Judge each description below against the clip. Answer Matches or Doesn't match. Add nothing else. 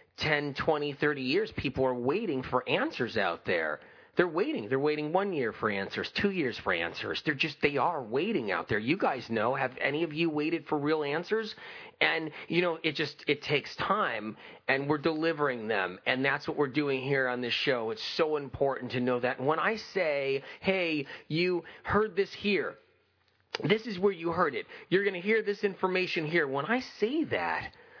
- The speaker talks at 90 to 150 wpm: Doesn't match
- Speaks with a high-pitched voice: Doesn't match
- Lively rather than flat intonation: Matches